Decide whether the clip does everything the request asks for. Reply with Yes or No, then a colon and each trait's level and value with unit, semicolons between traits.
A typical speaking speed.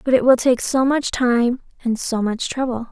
No: fast, 225 wpm